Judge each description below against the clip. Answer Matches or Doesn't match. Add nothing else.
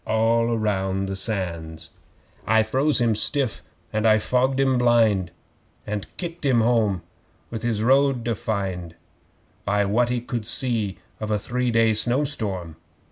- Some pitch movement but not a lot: Matches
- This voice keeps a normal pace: Matches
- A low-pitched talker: Matches